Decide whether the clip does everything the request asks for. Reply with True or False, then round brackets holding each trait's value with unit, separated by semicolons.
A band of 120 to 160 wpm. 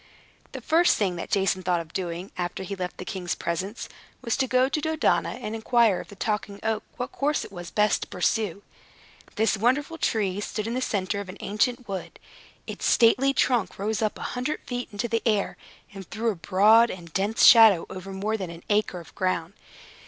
False (205 wpm)